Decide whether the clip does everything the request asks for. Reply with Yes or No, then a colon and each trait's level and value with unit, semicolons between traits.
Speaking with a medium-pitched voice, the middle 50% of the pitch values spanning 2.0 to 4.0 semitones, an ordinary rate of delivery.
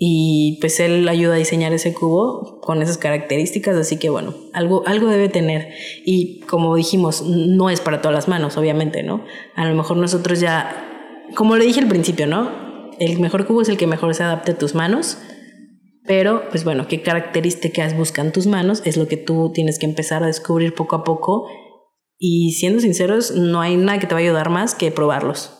No: medium, 170 Hz; narrow, 2.5 semitones; fast, 200 wpm